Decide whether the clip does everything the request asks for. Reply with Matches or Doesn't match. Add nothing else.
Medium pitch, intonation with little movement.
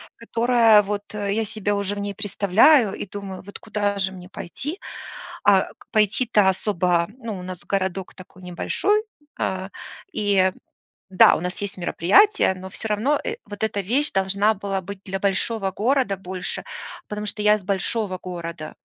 Doesn't match